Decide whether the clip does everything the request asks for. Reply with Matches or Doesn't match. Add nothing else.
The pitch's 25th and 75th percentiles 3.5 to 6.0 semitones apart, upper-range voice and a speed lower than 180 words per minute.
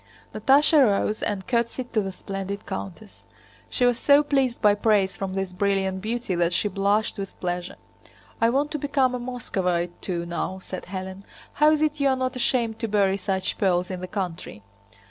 Doesn't match